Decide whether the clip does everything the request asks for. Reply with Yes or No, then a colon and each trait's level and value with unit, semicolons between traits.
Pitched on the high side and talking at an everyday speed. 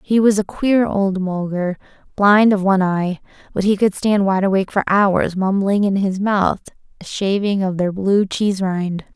Yes: high, 195 Hz; average, 190 wpm